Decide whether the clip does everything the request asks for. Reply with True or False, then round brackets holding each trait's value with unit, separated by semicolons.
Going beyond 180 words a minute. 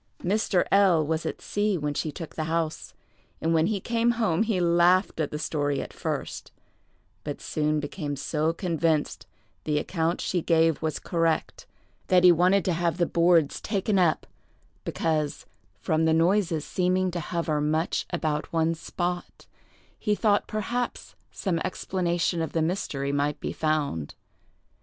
False (155 wpm)